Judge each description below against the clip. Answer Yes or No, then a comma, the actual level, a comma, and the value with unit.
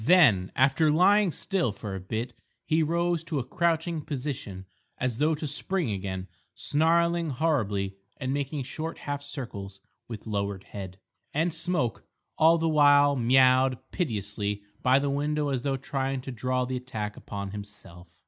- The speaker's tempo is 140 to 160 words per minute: Yes, average, 155 wpm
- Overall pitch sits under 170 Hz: Yes, low, 135 Hz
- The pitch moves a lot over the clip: Yes, wide, 7.0 semitones